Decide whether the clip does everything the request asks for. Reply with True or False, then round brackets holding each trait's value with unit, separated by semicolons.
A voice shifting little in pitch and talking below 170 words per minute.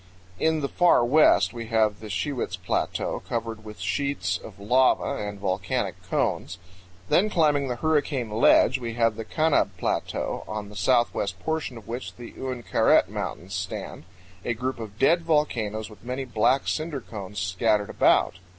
False (4.8 semitones; 160 wpm)